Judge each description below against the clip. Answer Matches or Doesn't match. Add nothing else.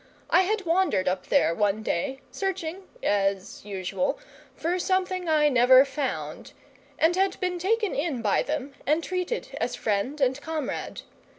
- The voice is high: Matches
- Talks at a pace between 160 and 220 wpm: Doesn't match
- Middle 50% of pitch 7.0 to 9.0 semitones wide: Matches